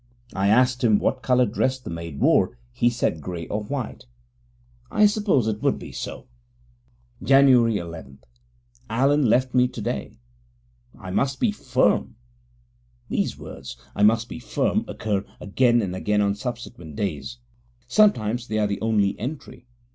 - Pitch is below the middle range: Yes, low, 115 Hz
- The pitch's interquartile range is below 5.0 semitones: Yes, average, 4.2 semitones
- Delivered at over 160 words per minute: No, average, 145 wpm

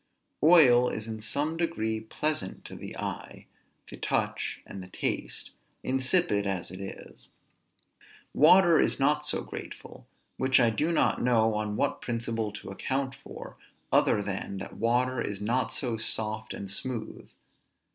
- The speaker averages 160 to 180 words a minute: No, average, 145 wpm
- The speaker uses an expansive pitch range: No, average, 4.2 semitones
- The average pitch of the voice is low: Yes, low, 115 Hz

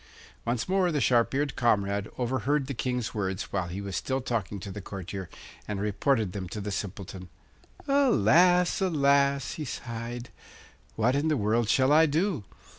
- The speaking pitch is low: Yes, low, 120 Hz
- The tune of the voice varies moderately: No, wide, 5.8 semitones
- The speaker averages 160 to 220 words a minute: Yes, average, 165 wpm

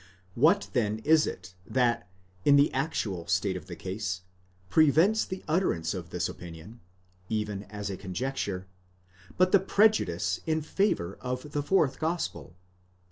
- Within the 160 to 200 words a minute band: No, average, 140 wpm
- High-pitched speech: No, low, 115 Hz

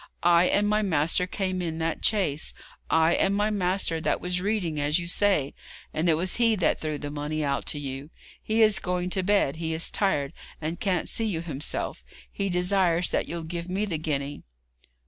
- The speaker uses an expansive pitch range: No, average, 3.8 semitones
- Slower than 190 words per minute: No, average, 200 wpm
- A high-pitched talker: No, medium, 175 Hz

